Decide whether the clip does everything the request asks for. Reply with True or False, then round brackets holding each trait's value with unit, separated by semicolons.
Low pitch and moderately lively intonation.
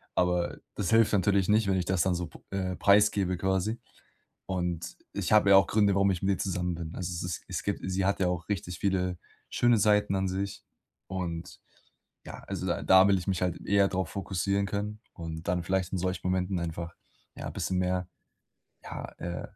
False (95 Hz; 1.9 semitones)